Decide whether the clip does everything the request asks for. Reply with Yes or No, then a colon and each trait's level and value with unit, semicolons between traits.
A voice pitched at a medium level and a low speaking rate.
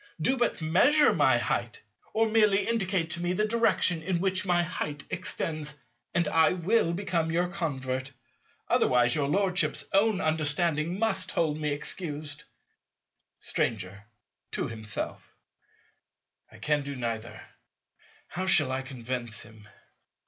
Yes: medium, 160 Hz; slow, 130 wpm